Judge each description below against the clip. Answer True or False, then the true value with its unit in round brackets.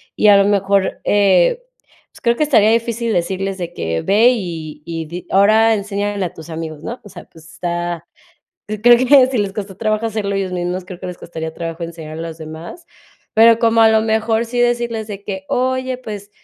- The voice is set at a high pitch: True (200 Hz)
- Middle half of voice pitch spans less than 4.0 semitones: False (4.7 semitones)